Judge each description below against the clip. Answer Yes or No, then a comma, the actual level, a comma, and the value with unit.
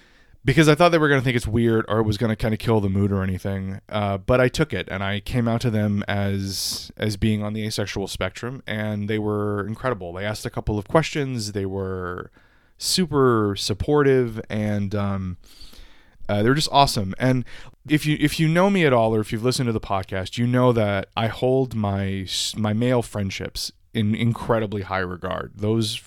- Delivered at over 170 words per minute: Yes, fast, 205 wpm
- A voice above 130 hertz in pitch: No, low, 110 Hz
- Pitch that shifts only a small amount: No, average, 3.9 semitones